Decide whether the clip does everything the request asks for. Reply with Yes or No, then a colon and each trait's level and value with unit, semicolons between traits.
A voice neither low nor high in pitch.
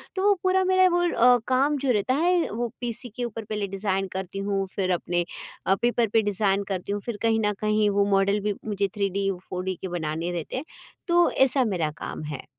No: high, 210 Hz